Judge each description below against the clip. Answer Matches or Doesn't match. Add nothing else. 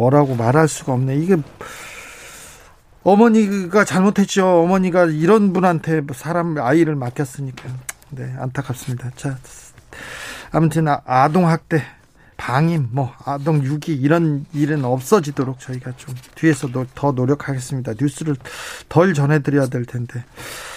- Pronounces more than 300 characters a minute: Doesn't match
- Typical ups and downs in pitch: Matches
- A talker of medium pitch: Matches